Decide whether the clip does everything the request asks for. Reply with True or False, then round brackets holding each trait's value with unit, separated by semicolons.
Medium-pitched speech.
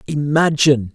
True (145 Hz)